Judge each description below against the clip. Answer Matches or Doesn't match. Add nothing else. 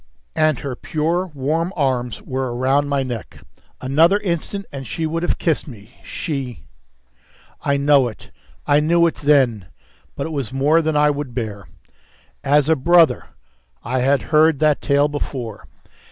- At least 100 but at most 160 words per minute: Matches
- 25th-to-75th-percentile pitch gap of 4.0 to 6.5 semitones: Doesn't match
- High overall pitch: Doesn't match